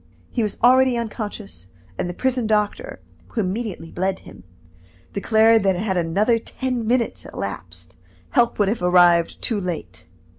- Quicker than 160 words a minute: No, average, 145 wpm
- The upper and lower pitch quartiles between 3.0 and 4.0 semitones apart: No, average, 4.5 semitones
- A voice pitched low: No, high, 210 Hz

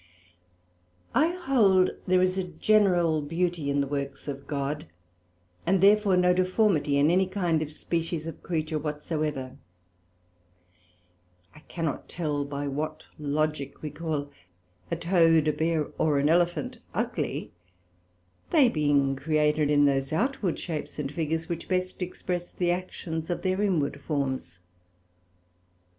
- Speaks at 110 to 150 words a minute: Yes, slow, 135 wpm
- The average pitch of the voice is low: No, medium, 160 Hz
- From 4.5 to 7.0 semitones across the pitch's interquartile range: No, average, 3.6 semitones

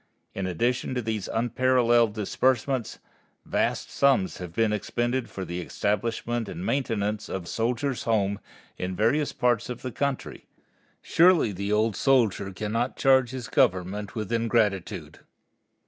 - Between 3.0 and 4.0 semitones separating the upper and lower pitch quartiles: Yes, average, 3.6 semitones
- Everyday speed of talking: No, slow, 130 wpm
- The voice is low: Yes, low, 115 Hz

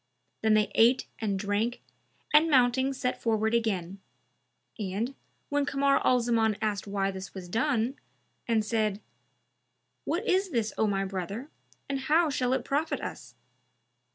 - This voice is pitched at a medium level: No, high, 230 Hz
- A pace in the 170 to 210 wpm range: No, average, 145 wpm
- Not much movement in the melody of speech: No, average, 4.8 semitones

